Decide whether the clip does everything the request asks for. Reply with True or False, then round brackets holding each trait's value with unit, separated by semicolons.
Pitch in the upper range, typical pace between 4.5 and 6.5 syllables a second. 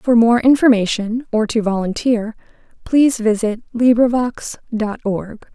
False (230 Hz; 4.3 syllables/s)